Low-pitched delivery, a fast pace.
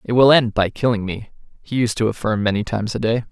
Yes: low, 110 Hz; fast, 255 wpm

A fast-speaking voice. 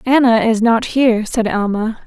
No: average, 175 wpm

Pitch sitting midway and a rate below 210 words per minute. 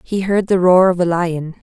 No: medium, 180 Hz; fast, 245 wpm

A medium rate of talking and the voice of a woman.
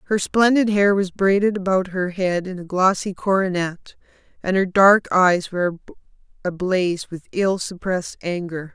Yes: average, 150 wpm; female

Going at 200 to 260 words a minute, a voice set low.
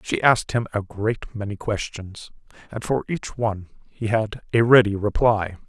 No: average, 170 wpm; low, 110 Hz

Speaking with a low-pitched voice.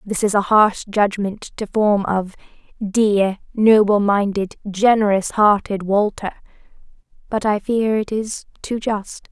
No: high, 205 Hz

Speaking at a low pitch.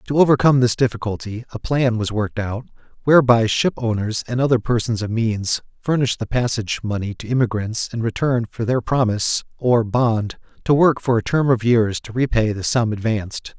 Yes: low, 115 Hz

